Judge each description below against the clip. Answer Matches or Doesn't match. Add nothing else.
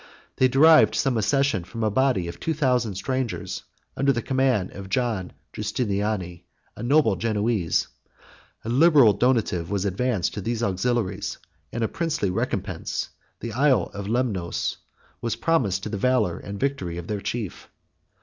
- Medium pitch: Doesn't match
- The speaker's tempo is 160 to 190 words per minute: Doesn't match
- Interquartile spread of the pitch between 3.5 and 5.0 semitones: Matches